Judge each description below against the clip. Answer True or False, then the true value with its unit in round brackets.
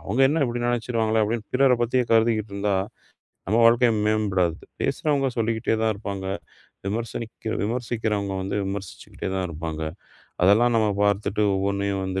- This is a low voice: True (110 Hz)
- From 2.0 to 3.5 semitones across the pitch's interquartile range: True (2.8 semitones)